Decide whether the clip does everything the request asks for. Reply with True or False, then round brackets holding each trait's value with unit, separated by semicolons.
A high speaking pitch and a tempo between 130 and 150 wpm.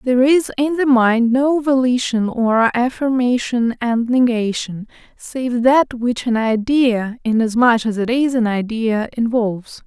True (240 Hz; 140 wpm)